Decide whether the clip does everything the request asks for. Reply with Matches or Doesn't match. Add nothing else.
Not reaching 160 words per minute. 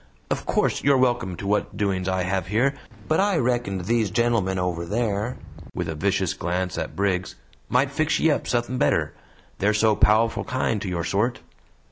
Doesn't match